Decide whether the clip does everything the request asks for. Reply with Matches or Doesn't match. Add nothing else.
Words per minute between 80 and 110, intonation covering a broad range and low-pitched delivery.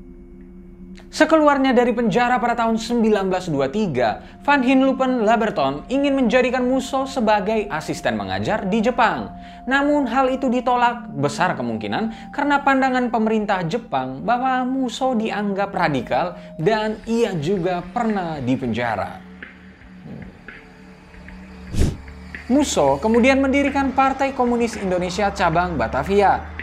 Doesn't match